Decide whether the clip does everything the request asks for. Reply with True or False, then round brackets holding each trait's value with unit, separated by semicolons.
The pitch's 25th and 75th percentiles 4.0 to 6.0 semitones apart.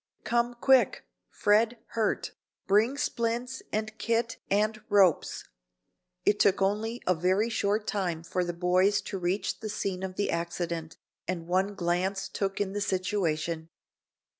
False (3.3 semitones)